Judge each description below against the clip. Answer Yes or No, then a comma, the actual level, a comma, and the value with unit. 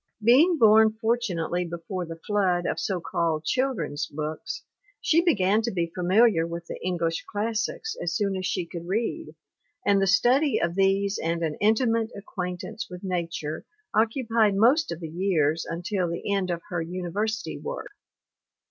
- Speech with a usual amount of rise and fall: Yes, average, 4.7 semitones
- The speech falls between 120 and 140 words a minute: No, average, 160 wpm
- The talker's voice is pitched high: Yes, high, 195 Hz